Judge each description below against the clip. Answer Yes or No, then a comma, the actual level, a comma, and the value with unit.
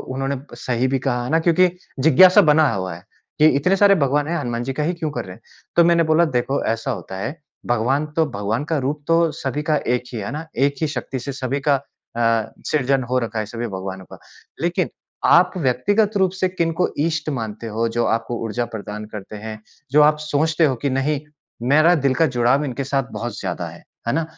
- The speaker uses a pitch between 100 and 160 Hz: Yes, low, 135 Hz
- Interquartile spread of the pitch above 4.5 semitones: Yes, average, 5.2 semitones